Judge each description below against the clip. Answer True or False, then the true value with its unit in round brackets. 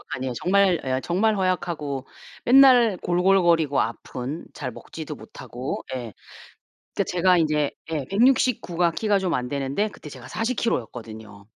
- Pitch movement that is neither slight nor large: False (6.8 semitones)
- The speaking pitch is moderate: True (165 Hz)